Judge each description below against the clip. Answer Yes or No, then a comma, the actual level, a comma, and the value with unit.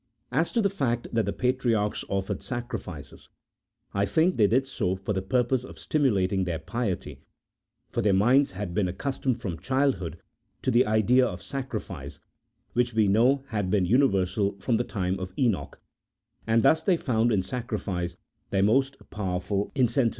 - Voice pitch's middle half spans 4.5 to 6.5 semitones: Yes, average, 5.0 semitones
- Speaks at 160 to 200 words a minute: Yes, average, 165 wpm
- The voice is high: No, low, 110 Hz